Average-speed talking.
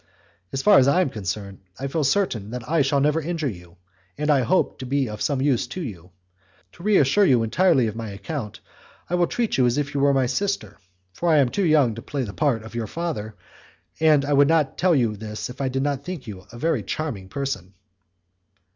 No: fast, 230 wpm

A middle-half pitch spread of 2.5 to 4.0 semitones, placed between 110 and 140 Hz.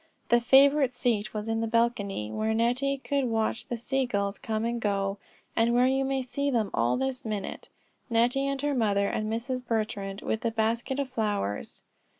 No: average, 3.2 semitones; high, 230 Hz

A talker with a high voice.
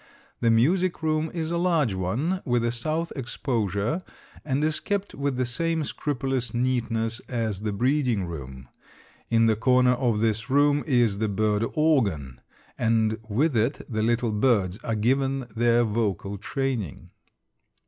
No: low, 120 Hz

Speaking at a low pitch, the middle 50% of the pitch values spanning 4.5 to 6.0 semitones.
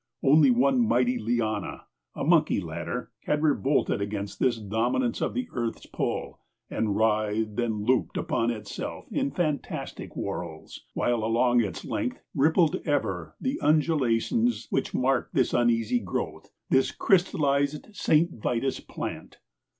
Yes: low, 125 Hz; average, 4.8 semitones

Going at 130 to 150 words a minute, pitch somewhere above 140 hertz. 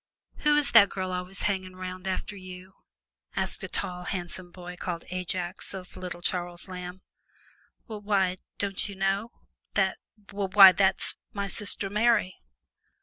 Yes: average, 145 wpm; medium, 185 Hz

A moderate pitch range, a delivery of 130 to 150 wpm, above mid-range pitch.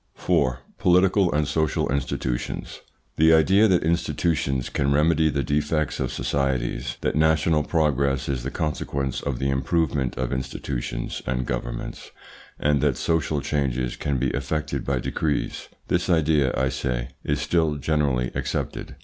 No: average, 3.1 semitones; average, 140 wpm; very low, 70 Hz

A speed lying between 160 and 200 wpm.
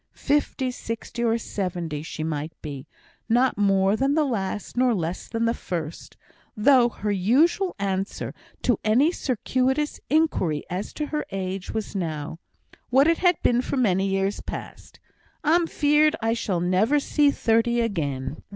No: average, 150 wpm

